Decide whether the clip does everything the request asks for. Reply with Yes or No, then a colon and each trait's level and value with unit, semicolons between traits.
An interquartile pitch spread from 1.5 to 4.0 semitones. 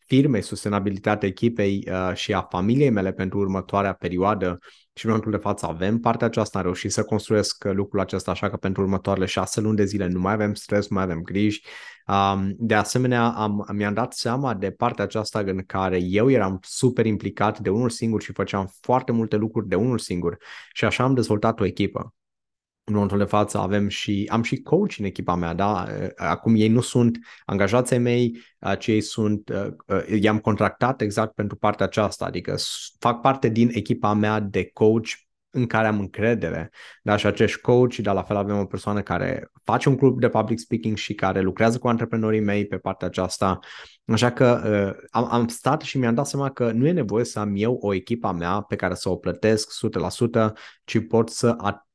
Yes: average, 2.8 semitones